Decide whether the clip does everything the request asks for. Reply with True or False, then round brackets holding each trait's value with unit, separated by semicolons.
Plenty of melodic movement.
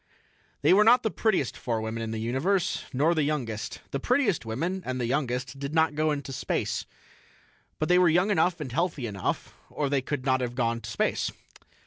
True (5.8 semitones)